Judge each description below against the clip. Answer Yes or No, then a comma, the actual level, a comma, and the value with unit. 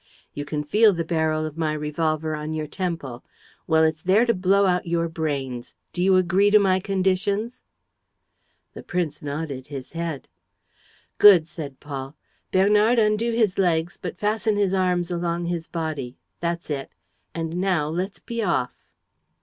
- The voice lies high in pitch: No, medium, 170 Hz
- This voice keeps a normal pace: Yes, average, 160 wpm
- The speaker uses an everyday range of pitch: Yes, average, 3.7 semitones